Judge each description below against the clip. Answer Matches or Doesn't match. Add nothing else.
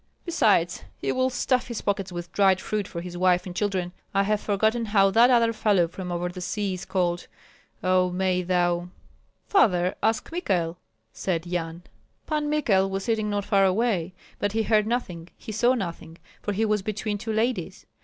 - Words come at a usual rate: Matches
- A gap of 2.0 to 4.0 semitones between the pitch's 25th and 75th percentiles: Matches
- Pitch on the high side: Matches